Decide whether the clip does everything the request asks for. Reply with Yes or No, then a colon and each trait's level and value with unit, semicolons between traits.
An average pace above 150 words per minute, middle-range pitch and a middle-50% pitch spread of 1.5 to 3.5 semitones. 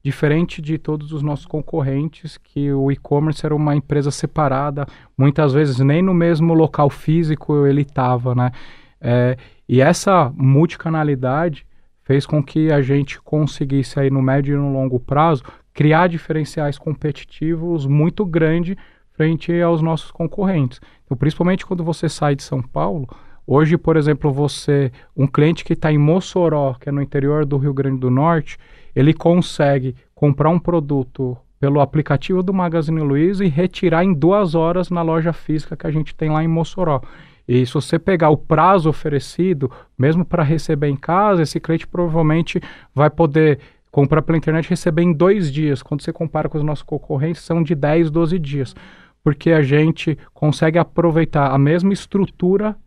Yes: average, 165 wpm; medium, 155 Hz; average, 2.8 semitones